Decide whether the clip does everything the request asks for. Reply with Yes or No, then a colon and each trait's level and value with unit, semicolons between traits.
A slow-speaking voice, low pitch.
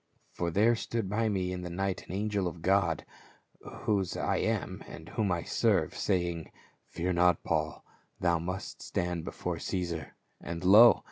No: average, 160 wpm; very low, 90 Hz